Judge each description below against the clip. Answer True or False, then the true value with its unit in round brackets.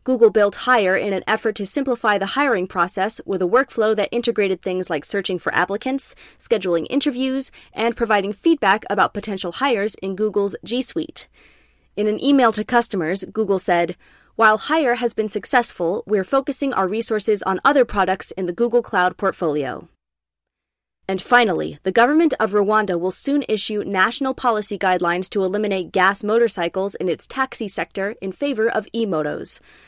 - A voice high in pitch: True (205 Hz)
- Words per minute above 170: False (165 wpm)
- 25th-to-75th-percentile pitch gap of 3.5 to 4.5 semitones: True (3.8 semitones)